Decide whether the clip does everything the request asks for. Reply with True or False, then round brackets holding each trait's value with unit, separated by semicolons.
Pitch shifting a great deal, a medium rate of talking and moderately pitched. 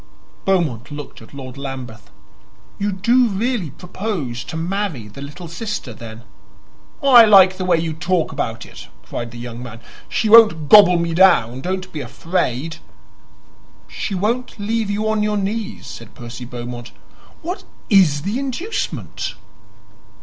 True (8.2 semitones; 145 wpm; 180 Hz)